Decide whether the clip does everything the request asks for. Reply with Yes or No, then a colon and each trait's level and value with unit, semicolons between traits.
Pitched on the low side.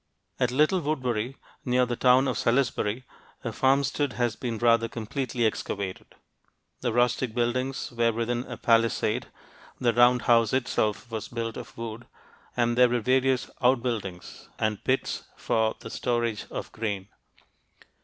Yes: low, 120 Hz